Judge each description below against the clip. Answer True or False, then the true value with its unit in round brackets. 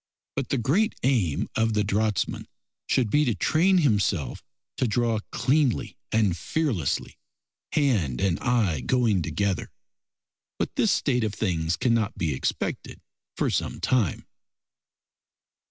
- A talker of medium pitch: False (110 Hz)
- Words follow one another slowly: True (125 wpm)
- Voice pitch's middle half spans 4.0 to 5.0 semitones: False (5.5 semitones)